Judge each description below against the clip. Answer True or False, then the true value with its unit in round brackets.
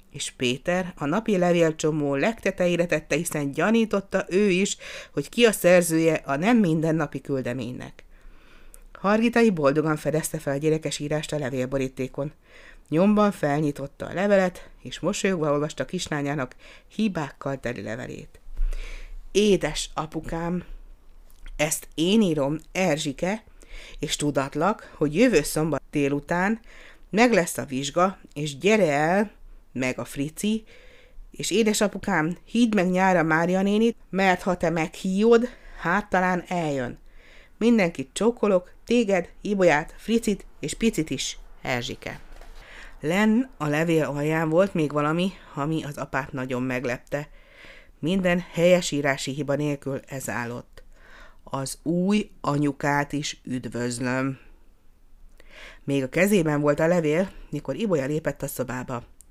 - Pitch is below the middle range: False (155 Hz)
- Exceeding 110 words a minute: True (120 wpm)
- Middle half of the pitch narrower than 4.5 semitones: False (5.3 semitones)